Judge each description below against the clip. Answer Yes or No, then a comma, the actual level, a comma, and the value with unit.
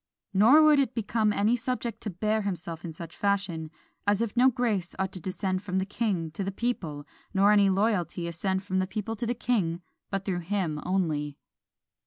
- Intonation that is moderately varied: Yes, average, 3.9 semitones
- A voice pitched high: Yes, high, 195 Hz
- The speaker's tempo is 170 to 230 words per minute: Yes, average, 200 wpm